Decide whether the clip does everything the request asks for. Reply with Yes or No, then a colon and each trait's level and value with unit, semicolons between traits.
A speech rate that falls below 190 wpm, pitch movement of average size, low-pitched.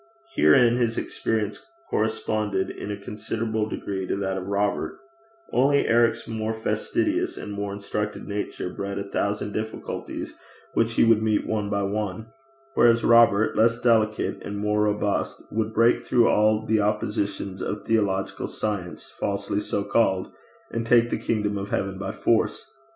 No: average, 150 wpm; narrow, 1.9 semitones; low, 105 Hz